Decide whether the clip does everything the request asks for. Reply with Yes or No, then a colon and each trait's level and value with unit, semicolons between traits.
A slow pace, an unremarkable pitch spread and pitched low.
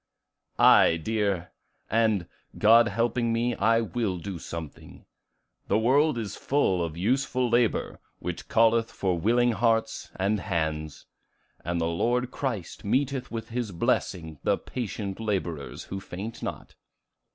Yes: slow, 130 wpm; average, 4.8 semitones; low, 110 Hz